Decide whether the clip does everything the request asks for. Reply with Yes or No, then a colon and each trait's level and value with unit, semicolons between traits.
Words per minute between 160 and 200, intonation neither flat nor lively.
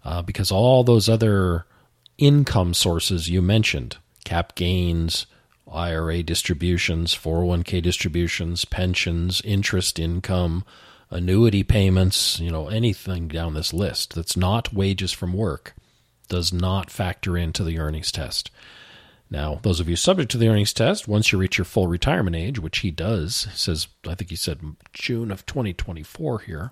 No: average, 150 wpm; average, 3.6 semitones